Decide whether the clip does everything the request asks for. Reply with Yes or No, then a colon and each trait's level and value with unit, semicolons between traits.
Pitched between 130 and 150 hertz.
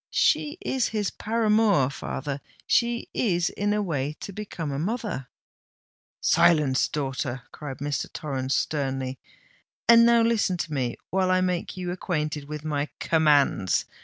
No: medium, 160 Hz